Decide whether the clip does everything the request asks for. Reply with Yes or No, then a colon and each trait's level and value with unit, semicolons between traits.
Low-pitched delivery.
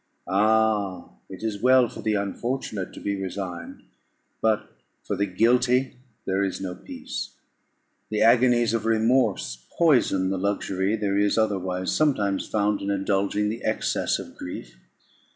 Yes: low, 105 Hz